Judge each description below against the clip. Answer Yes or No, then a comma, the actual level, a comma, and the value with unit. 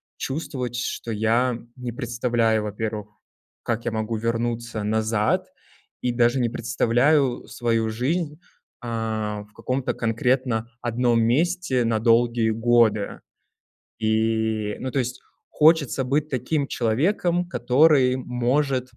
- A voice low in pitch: Yes, low, 120 Hz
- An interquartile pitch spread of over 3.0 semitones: No, narrow, 2.5 semitones